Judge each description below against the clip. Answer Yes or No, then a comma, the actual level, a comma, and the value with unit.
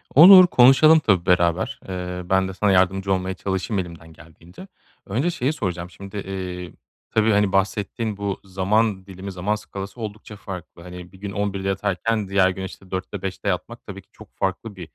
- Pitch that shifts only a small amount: Yes, narrow, 2.2 semitones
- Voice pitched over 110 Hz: No, very low, 95 Hz